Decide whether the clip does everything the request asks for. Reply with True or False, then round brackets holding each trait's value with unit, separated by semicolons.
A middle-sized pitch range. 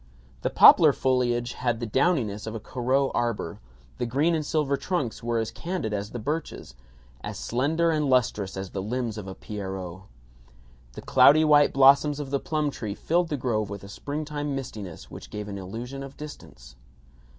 False (5.7 semitones)